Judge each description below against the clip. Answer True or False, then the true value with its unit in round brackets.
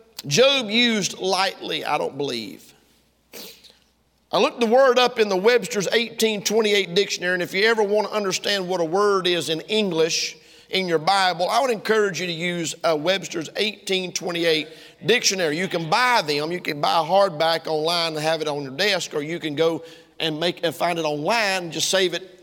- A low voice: False (180 Hz)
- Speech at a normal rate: True (195 wpm)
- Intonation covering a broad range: False (4.0 semitones)